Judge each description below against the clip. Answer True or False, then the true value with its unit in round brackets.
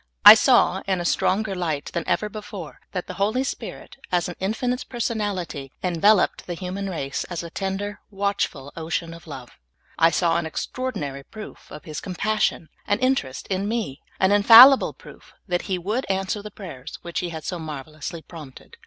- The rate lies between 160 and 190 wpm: True (175 wpm)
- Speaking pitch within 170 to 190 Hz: True (185 Hz)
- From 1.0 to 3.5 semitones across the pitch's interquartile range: False (4.0 semitones)